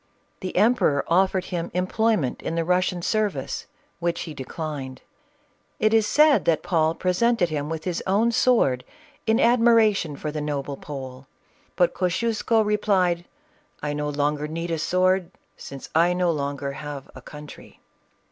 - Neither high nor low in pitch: Yes, medium, 170 Hz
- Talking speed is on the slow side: No, average, 145 wpm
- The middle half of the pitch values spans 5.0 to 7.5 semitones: Yes, average, 5.3 semitones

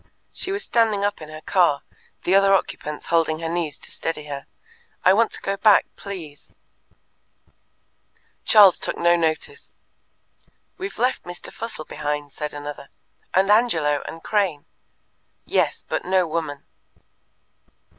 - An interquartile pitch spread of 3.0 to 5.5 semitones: Yes, average, 5.0 semitones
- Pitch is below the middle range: No, medium, 170 Hz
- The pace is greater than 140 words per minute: No, slow, 135 wpm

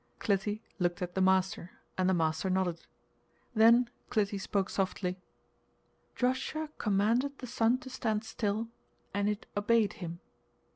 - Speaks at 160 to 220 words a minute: No, slow, 135 wpm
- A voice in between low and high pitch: No, high, 205 Hz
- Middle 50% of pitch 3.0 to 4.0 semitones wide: Yes, average, 3.3 semitones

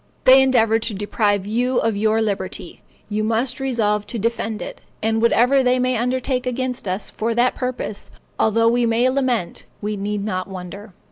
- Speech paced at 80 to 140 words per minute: No, average, 175 wpm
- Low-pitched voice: No, high, 225 Hz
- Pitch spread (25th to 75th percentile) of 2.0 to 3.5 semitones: Yes, average, 3.1 semitones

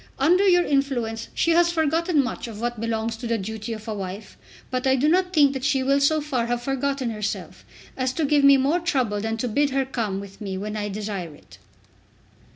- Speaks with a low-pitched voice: No, very high, 255 Hz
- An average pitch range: Yes, average, 4.5 semitones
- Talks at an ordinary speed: No, fast, 220 wpm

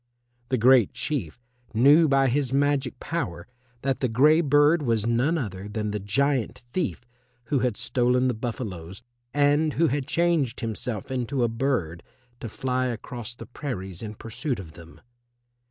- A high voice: No, low, 125 Hz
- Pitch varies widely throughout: No, average, 4.4 semitones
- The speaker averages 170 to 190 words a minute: No, average, 155 wpm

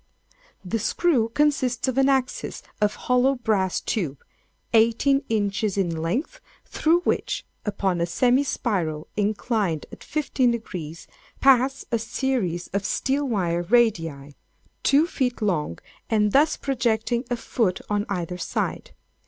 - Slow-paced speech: Yes, slow, 130 wpm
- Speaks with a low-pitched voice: No, high, 225 Hz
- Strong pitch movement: Yes, wide, 5.9 semitones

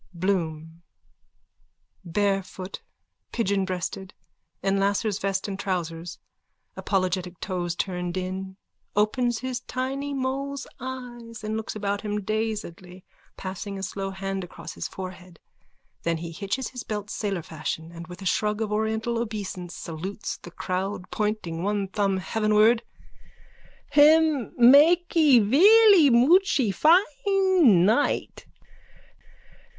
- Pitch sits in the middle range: No, high, 205 Hz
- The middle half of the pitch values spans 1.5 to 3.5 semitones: No, average, 4.7 semitones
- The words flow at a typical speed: No, slow, 115 wpm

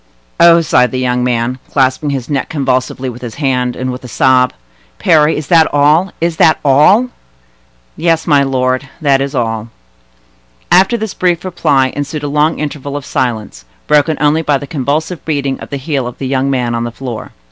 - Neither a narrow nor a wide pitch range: Yes, average, 3.3 semitones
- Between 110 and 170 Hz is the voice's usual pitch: Yes, medium, 140 Hz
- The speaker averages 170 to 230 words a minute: Yes, average, 185 wpm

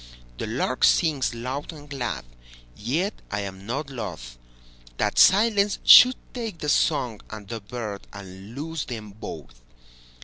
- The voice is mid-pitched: No, low, 115 Hz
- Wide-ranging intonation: Yes, wide, 7.6 semitones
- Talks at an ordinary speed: No, slow, 125 wpm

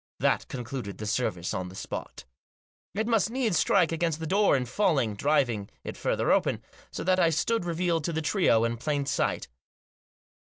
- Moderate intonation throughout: No, wide, 7.4 semitones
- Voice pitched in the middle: Yes, medium, 155 Hz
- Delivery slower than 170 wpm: No, average, 180 wpm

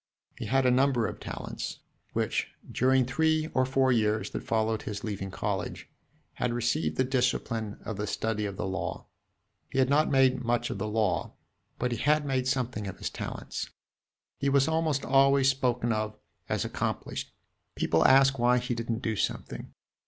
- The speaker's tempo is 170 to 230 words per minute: Yes, average, 175 wpm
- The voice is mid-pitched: No, low, 125 Hz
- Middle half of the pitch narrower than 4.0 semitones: Yes, average, 3.4 semitones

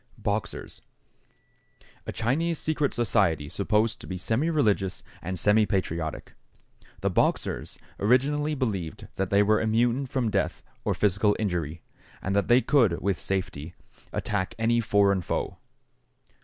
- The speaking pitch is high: No, low, 105 Hz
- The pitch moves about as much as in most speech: Yes, average, 4.0 semitones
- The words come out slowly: Yes, slow, 125 wpm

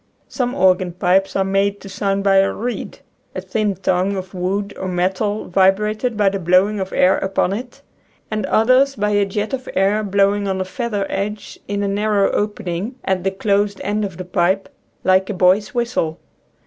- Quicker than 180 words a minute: Yes, average, 200 wpm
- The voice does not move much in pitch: Yes, narrow, 1.9 semitones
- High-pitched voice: Yes, high, 200 Hz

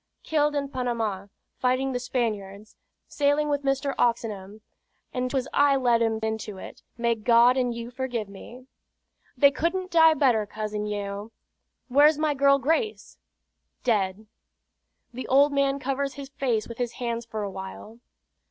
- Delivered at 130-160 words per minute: Yes, average, 150 wpm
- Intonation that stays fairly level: No, average, 4.2 semitones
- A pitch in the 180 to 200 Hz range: No, high, 245 Hz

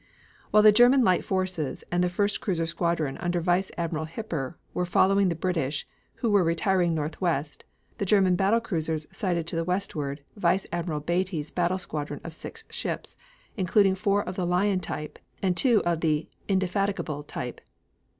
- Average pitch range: Yes, average, 3.0 semitones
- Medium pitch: Yes, medium, 180 Hz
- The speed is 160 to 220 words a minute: Yes, average, 170 wpm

